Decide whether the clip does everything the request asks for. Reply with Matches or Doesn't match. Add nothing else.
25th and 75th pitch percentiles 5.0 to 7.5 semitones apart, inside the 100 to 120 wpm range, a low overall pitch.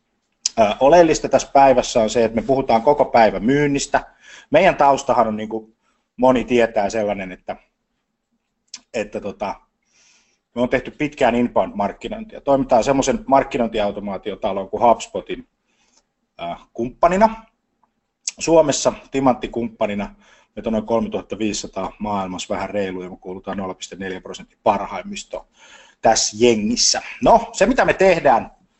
Matches